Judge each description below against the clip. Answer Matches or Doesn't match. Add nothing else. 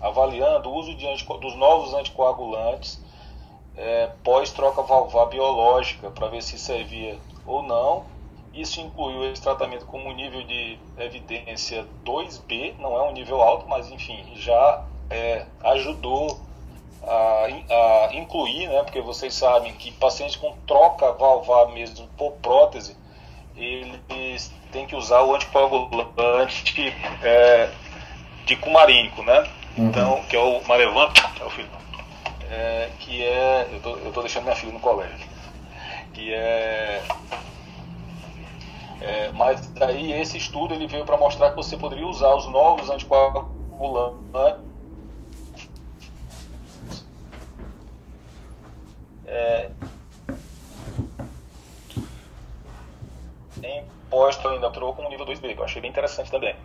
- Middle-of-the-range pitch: Doesn't match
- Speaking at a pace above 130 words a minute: Doesn't match